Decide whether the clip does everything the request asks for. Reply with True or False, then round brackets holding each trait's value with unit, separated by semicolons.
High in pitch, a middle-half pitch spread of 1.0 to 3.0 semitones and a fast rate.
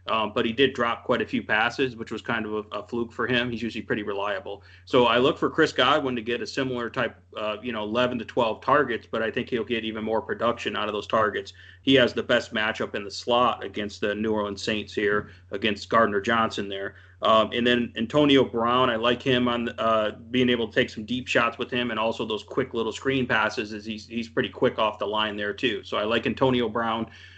False (115 Hz; 2.4 semitones; 245 wpm)